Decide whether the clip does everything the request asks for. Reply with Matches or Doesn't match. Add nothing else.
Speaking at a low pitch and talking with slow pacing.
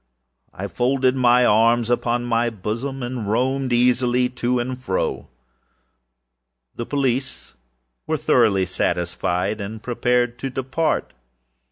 Matches